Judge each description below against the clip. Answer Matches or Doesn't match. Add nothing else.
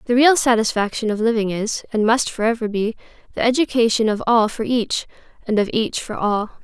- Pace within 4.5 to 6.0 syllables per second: Matches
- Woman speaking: Matches